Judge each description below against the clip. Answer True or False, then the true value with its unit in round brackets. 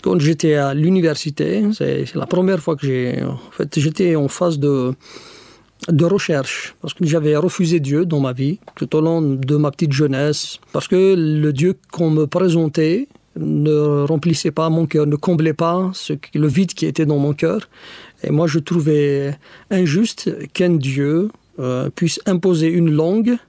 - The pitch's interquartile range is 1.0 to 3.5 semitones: True (3.1 semitones)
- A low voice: False (160 Hz)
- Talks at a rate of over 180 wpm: False (175 wpm)